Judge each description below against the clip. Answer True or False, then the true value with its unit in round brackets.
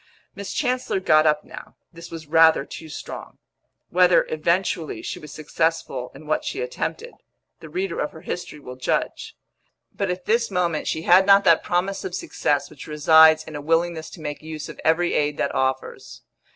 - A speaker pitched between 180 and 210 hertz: False (165 Hz)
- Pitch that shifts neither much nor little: True (3.1 semitones)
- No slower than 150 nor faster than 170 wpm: False (180 wpm)